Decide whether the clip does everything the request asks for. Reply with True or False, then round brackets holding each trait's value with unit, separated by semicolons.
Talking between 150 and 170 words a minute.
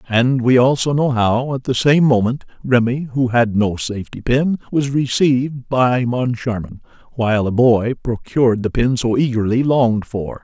True (165 wpm)